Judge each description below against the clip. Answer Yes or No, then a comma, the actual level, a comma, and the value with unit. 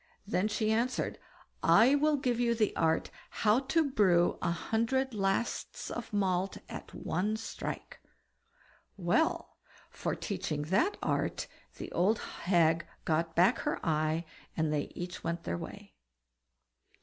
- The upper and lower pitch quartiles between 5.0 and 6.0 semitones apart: Yes, wide, 5.6 semitones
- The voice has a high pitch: Yes, high, 195 Hz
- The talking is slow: Yes, slow, 130 wpm